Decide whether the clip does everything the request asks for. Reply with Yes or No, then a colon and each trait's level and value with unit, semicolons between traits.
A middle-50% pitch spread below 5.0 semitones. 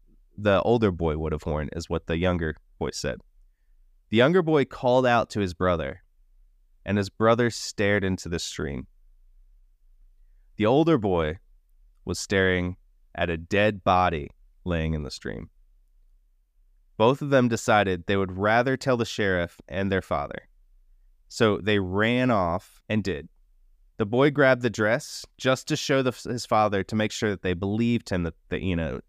No: average, 5.3 semitones